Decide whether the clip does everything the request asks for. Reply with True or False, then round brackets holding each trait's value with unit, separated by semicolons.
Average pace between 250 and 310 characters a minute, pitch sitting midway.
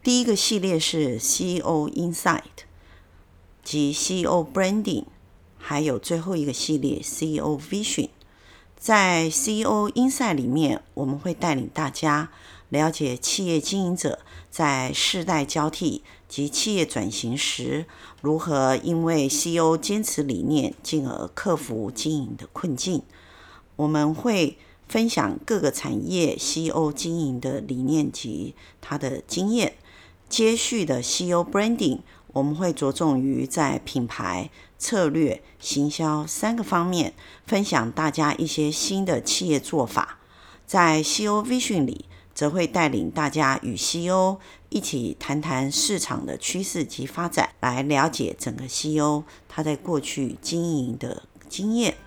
False (240 characters per minute; 155 Hz)